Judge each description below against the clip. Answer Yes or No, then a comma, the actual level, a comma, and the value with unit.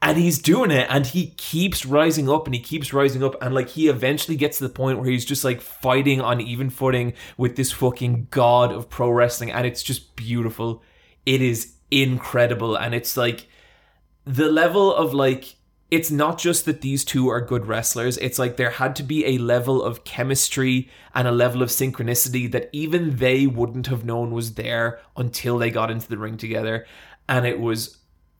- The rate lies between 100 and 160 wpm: No, average, 195 wpm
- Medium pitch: No, low, 125 Hz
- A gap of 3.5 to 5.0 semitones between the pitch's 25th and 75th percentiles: No, narrow, 2.5 semitones